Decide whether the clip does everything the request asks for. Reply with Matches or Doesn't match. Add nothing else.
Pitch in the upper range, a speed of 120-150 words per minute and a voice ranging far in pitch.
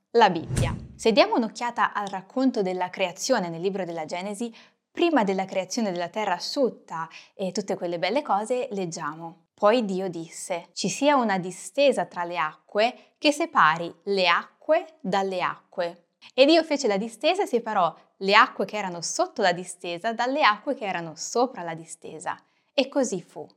Doesn't match